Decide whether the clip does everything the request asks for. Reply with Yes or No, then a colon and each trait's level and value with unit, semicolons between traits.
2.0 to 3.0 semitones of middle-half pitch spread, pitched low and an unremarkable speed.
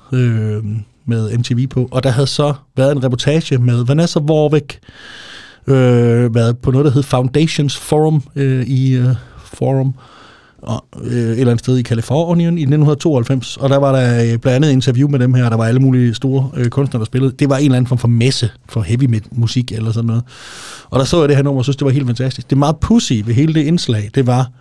No: narrow, 2.6 semitones; low, 130 Hz; fast, 230 wpm